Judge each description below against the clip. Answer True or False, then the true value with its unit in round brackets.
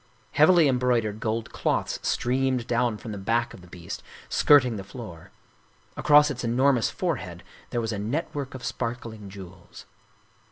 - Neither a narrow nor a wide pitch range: True (3.6 semitones)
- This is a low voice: True (120 Hz)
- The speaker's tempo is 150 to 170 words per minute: True (155 wpm)